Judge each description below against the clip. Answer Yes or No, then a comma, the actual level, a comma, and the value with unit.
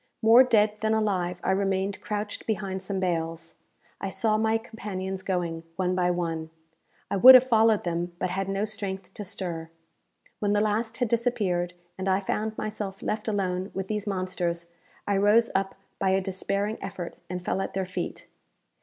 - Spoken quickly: No, average, 175 wpm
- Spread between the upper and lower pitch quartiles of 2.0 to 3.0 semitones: Yes, average, 2.7 semitones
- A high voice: Yes, high, 195 Hz